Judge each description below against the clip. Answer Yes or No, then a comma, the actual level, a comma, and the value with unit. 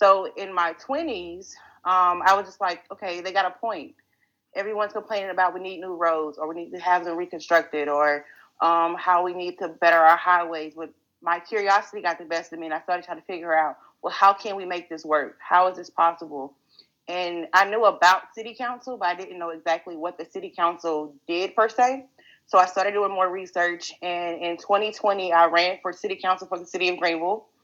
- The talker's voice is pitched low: No, medium, 180 Hz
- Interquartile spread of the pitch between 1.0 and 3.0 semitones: Yes, narrow, 2.6 semitones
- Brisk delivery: Yes, fast, 215 wpm